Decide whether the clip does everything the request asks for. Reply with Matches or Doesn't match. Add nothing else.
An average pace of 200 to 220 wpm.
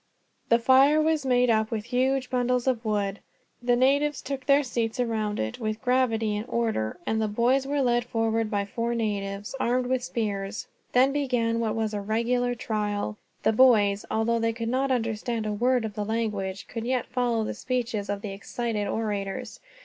Doesn't match